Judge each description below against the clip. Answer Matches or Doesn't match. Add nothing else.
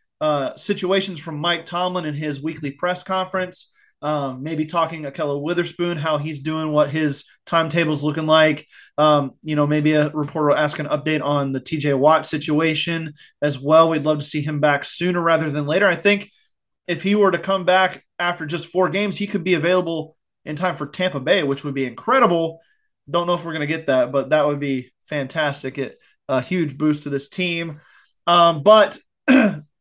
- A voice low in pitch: Doesn't match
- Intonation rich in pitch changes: Doesn't match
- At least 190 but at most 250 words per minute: Matches